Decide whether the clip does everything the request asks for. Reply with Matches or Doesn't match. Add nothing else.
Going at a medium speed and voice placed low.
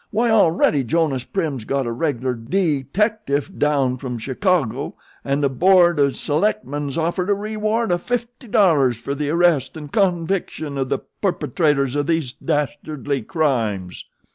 Doesn't match